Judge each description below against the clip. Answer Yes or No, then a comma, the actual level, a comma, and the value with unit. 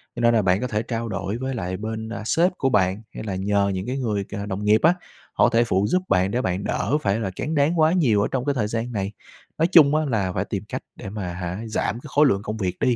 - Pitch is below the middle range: Yes, low, 110 Hz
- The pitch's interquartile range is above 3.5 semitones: Yes, average, 4.7 semitones